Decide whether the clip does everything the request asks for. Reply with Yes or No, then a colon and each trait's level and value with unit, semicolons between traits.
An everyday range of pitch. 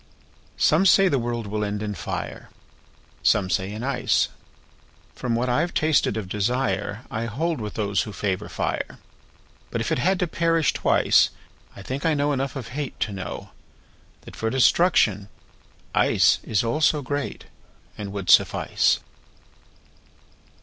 No: wide, 5.8 semitones